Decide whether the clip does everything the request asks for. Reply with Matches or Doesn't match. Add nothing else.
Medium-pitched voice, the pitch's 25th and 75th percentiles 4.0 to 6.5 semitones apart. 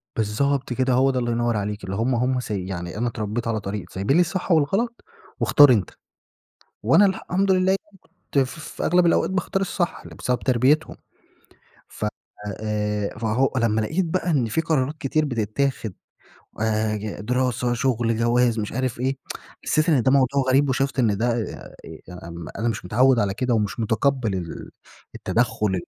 Doesn't match